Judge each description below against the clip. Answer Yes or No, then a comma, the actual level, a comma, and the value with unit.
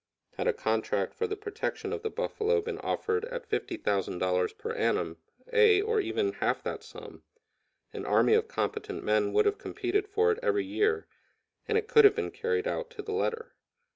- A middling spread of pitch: No, narrow, 1.7 semitones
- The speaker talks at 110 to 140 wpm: No, average, 185 wpm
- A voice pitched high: Yes, very high, 430 Hz